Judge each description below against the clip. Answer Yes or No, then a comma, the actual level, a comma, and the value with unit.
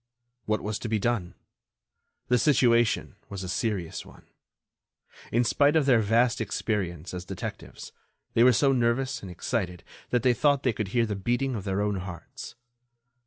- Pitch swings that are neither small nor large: Yes, average, 4.0 semitones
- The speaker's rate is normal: Yes, average, 165 wpm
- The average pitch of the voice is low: Yes, low, 115 Hz